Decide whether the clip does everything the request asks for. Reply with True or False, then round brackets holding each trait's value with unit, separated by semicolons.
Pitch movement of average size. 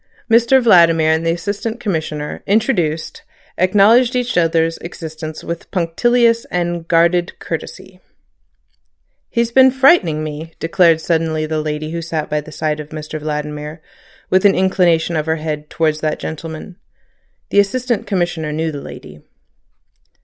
True (4.2 semitones)